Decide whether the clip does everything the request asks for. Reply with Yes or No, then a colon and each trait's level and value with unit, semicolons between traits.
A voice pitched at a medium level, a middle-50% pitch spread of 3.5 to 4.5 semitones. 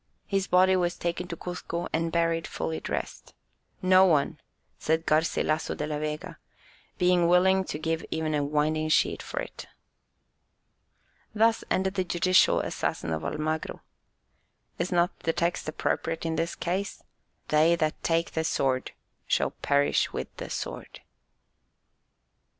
No: medium, 165 Hz; narrow, 2.5 semitones